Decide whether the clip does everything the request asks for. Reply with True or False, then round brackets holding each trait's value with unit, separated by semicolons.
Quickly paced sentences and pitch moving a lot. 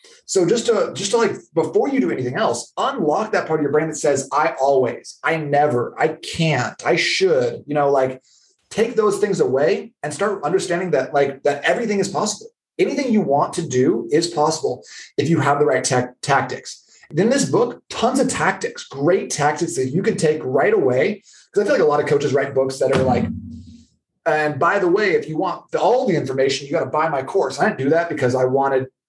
True (220 wpm; 6.7 semitones)